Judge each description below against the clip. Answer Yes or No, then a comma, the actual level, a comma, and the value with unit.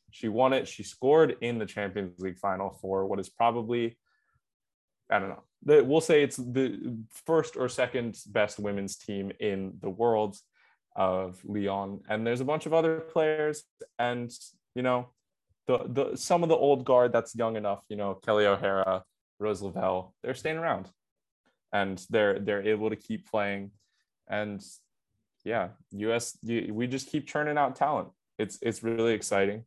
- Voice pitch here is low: Yes, low, 110 Hz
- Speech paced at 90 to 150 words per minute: No, average, 165 wpm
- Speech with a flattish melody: No, average, 4.2 semitones